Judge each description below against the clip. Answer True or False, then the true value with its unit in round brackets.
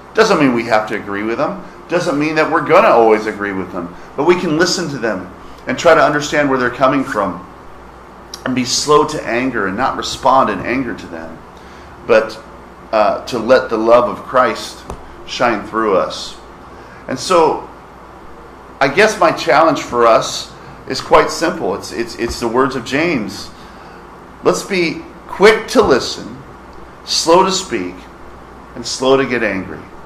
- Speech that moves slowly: False (170 wpm)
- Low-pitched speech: True (115 Hz)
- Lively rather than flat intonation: True (7.1 semitones)